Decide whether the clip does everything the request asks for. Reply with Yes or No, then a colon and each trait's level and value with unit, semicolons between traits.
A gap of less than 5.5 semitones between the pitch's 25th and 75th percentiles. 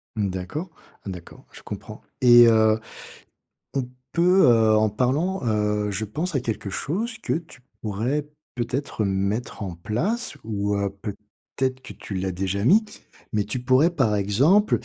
No: wide, 5.8 semitones